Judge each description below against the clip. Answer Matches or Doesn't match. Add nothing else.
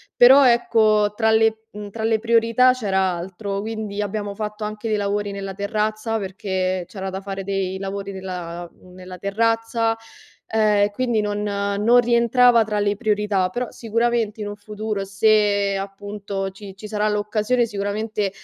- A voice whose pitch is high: Matches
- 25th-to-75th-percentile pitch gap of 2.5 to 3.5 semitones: Doesn't match